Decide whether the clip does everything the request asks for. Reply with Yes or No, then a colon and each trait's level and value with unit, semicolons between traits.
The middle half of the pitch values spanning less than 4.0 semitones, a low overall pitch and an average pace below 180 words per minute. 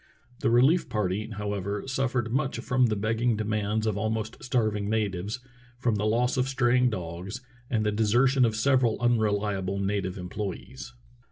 Yes: average, 3.1 semitones; low, 110 Hz; average, 155 wpm